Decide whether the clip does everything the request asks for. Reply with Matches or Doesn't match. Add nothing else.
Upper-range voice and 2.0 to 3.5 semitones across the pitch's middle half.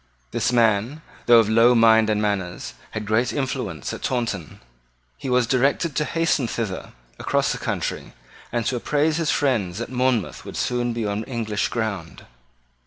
Doesn't match